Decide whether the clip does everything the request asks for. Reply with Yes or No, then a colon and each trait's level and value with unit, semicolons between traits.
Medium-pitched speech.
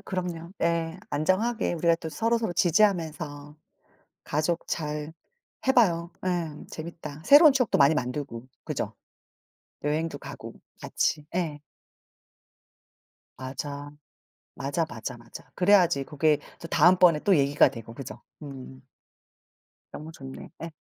Yes: medium, 160 Hz